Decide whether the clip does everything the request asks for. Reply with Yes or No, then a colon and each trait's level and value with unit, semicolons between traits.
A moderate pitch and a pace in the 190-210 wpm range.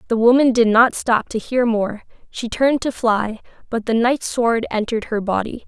No: high, 230 Hz; average, 200 wpm